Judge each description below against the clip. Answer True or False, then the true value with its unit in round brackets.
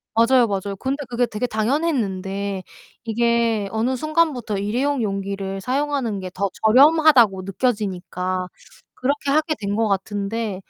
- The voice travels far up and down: False (4.8 semitones)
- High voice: True (220 Hz)